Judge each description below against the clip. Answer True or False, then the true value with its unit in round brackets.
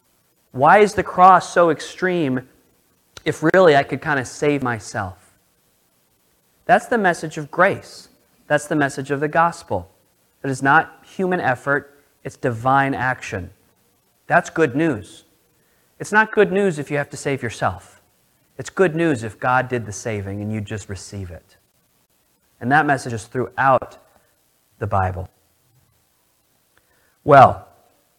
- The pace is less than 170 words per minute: True (145 wpm)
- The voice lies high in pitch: False (130 Hz)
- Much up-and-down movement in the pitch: True (7.3 semitones)